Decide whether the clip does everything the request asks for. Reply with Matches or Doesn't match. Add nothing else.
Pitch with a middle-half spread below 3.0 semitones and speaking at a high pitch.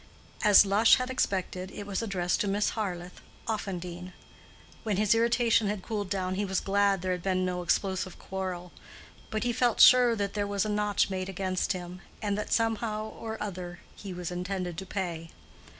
Matches